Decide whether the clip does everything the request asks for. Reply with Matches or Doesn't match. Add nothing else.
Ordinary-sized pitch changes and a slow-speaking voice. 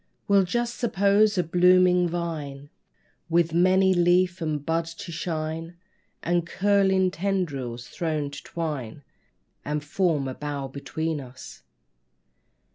Matches